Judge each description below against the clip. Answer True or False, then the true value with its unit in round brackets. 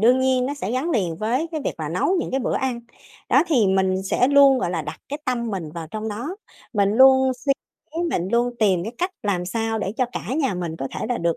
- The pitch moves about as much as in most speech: False (5.8 semitones)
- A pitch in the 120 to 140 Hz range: False (230 Hz)